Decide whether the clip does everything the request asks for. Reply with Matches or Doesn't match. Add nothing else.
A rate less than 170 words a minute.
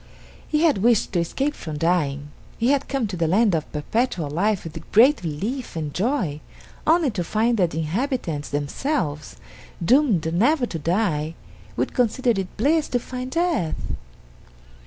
Matches